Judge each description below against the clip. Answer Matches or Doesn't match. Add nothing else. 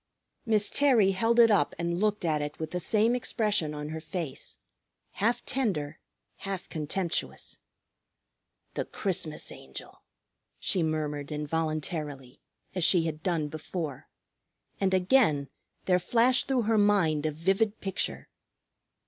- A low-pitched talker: Doesn't match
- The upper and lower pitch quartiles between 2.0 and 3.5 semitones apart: Doesn't match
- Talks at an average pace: Doesn't match